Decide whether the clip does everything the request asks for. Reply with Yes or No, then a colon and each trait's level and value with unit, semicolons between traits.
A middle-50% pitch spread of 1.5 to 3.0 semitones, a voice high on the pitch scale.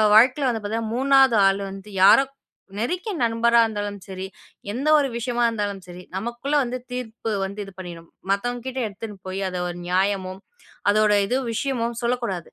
No: average, 3.9 semitones; high, 225 Hz